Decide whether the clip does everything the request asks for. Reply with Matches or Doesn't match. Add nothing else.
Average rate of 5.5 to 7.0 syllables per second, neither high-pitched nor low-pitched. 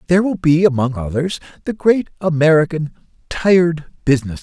Matches